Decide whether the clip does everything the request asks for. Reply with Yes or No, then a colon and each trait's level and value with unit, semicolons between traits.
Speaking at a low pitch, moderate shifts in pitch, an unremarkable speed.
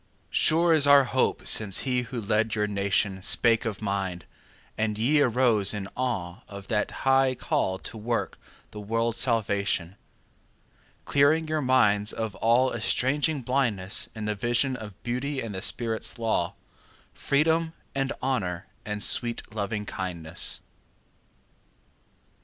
No: low, 115 Hz; average, 4.3 semitones; slow, 120 wpm